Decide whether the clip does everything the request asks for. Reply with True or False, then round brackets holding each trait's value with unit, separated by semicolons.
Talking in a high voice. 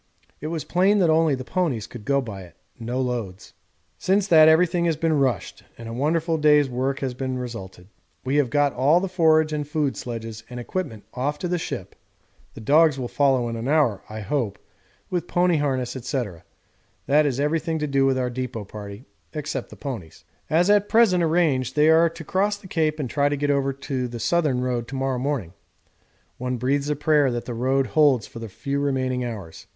False (140 Hz)